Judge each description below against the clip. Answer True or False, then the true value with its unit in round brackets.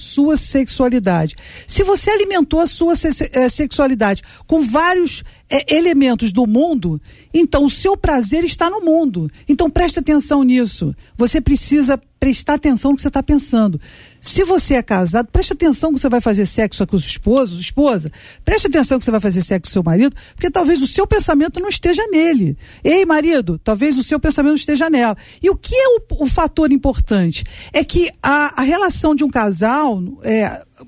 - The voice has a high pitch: True (285 Hz)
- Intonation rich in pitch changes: True (5.7 semitones)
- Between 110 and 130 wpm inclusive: False (180 wpm)